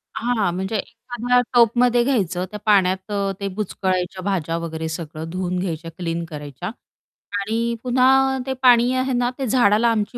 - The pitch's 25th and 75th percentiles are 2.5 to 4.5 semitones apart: No, average, 5.3 semitones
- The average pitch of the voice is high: Yes, high, 205 Hz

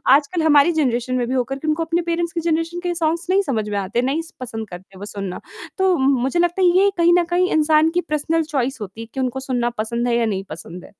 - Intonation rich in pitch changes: Yes, wide, 6.0 semitones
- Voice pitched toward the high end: Yes, very high, 285 Hz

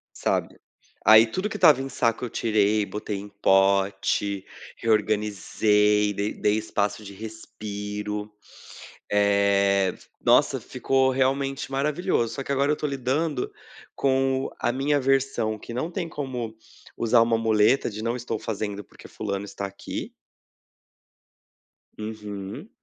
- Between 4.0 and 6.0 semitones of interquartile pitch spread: Yes, average, 4.4 semitones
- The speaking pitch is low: Yes, low, 110 Hz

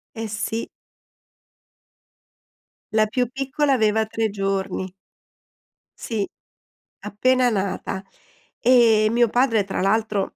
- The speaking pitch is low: No, high, 220 Hz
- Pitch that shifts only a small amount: No, average, 3.1 semitones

